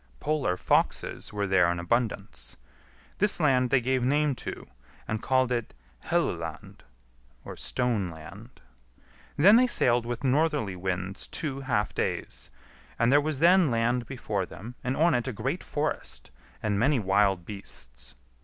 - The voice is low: Yes, low, 120 Hz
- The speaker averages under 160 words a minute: Yes, average, 145 wpm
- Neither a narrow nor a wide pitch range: No, wide, 5.7 semitones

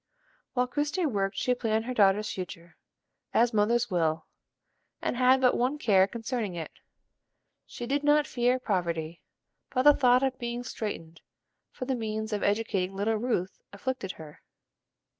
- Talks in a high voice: Yes, high, 225 Hz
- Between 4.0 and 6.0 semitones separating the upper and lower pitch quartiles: Yes, average, 4.7 semitones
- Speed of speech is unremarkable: Yes, average, 150 wpm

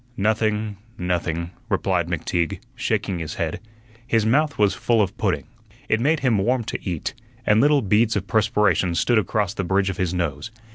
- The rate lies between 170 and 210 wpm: Yes, average, 175 wpm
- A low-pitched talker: Yes, low, 105 Hz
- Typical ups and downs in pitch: Yes, average, 4.0 semitones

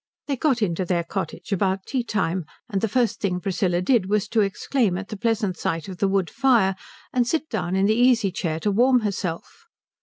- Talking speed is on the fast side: Yes, fast, 210 wpm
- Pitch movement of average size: Yes, average, 4.1 semitones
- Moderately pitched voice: No, high, 200 Hz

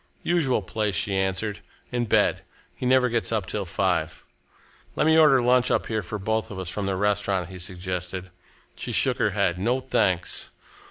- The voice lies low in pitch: Yes, low, 100 Hz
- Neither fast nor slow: Yes, average, 180 wpm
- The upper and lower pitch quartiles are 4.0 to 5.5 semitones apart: Yes, average, 4.4 semitones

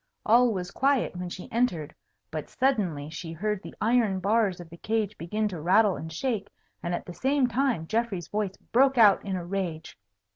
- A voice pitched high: Yes, high, 200 Hz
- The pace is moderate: Yes, average, 185 wpm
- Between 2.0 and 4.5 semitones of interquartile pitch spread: No, average, 4.9 semitones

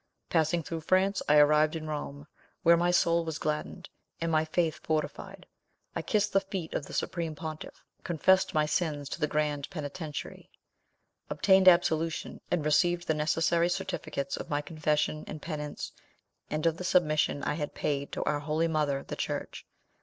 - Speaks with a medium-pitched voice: Yes, medium, 155 Hz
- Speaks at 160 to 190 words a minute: Yes, average, 170 wpm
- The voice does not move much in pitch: Yes, narrow, 2.3 semitones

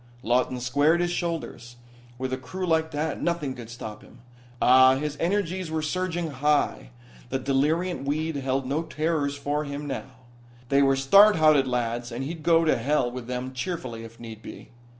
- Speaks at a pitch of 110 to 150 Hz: Yes, medium, 140 Hz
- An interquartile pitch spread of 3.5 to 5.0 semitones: Yes, average, 4.1 semitones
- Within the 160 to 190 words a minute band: Yes, average, 175 wpm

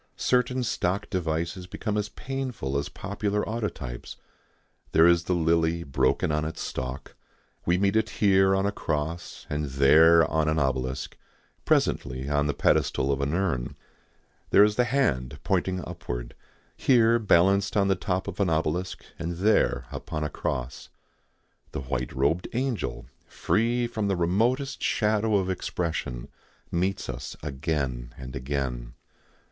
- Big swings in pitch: Yes, wide, 6.5 semitones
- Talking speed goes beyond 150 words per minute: No, average, 145 wpm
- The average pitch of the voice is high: No, very low, 85 Hz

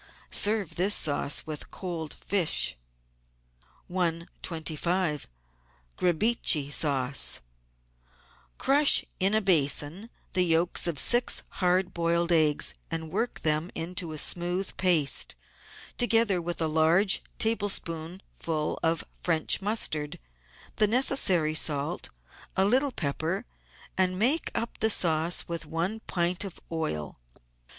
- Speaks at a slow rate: Yes, slow, 110 wpm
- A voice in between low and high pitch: Yes, medium, 175 Hz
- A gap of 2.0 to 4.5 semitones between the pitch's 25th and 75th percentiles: Yes, average, 3.7 semitones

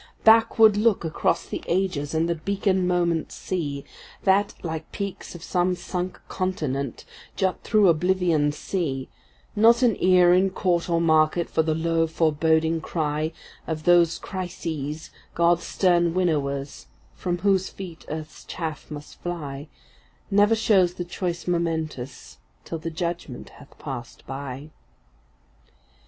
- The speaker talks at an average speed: No, slow, 130 wpm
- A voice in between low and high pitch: Yes, medium, 170 Hz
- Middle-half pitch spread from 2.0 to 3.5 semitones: Yes, average, 3.0 semitones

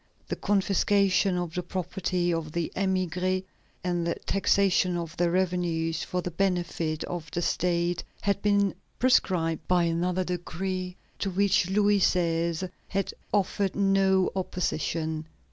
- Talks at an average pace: No, slow, 130 wpm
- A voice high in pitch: No, medium, 180 Hz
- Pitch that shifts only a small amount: Yes, narrow, 2.2 semitones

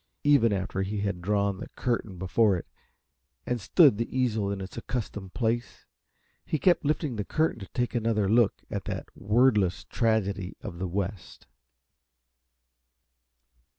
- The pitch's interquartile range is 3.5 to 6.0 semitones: Yes, average, 3.8 semitones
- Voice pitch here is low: Yes, low, 105 Hz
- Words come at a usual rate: Yes, average, 145 wpm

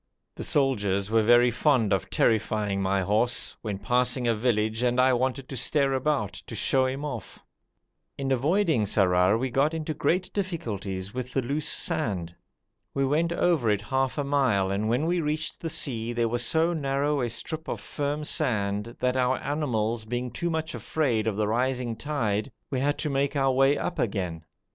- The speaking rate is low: No, average, 185 wpm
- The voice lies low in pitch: Yes, low, 125 Hz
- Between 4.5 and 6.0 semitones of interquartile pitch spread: Yes, average, 4.8 semitones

